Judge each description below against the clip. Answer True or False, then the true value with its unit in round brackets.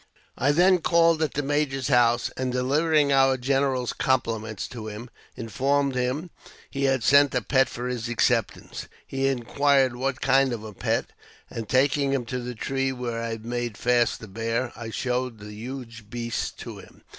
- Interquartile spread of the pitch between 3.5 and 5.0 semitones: False (2.6 semitones)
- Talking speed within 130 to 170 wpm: False (180 wpm)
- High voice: False (125 Hz)